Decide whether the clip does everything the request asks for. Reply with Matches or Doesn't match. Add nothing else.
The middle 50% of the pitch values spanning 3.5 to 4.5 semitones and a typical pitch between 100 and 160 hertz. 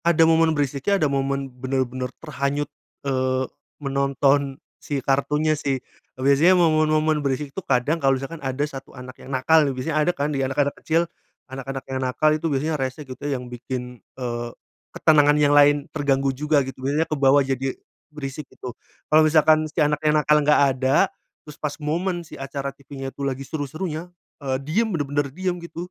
Doesn't match